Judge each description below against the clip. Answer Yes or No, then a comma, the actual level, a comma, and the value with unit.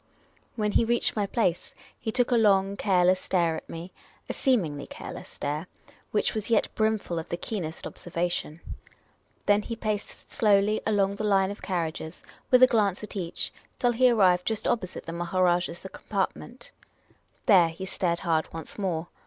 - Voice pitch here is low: No, high, 195 Hz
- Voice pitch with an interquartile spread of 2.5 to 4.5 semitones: Yes, average, 3.9 semitones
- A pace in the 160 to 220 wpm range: Yes, average, 170 wpm